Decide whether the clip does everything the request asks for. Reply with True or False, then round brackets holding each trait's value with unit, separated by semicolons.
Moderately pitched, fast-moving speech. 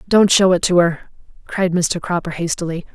False (175 Hz; 185 wpm)